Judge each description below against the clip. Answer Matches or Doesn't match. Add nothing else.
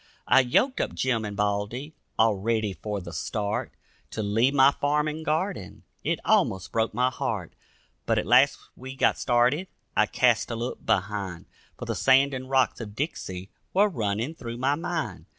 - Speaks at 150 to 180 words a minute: Matches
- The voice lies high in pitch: Doesn't match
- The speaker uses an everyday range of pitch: Matches